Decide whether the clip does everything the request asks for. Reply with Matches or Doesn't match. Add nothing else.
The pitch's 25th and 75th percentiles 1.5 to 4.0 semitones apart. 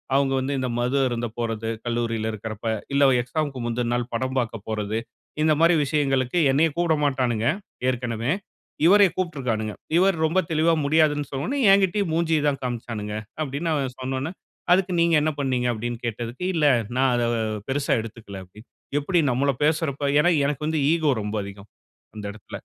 Doesn't match